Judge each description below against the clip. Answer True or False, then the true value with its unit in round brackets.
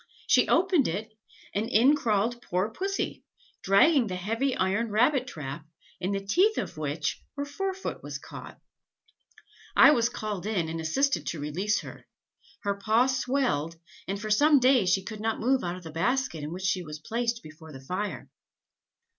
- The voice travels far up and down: True (6.2 semitones)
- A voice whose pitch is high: True (210 Hz)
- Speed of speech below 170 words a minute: False (175 wpm)